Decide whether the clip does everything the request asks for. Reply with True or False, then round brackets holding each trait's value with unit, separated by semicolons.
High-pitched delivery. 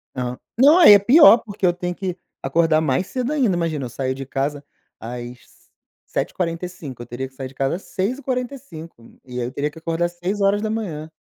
False (170 Hz)